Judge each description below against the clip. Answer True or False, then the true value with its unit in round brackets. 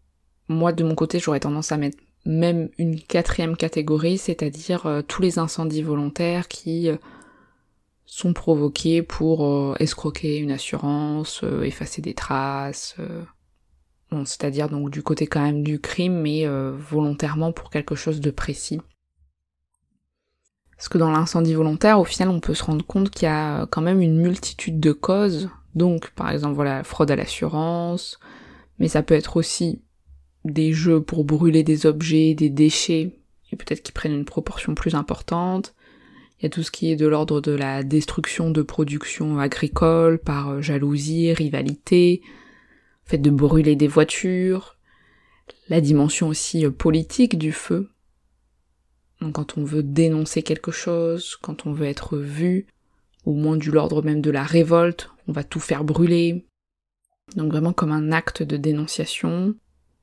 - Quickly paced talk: False (155 wpm)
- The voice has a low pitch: False (155 Hz)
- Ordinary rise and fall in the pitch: False (2.2 semitones)